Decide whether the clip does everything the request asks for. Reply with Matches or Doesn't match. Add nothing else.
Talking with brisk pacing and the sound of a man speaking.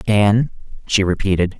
Doesn't match